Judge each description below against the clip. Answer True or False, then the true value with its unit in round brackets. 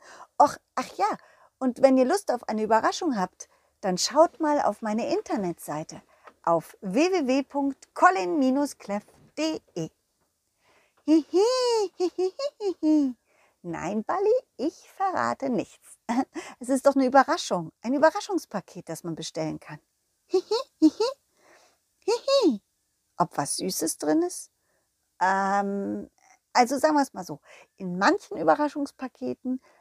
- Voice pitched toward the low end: False (275 Hz)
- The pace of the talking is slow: True (115 wpm)